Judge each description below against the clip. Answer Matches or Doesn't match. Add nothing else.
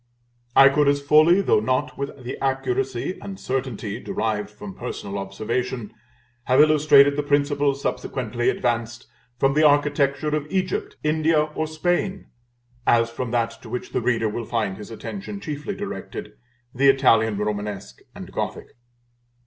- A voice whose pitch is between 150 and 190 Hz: Doesn't match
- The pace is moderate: Matches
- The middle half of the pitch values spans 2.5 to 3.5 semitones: Doesn't match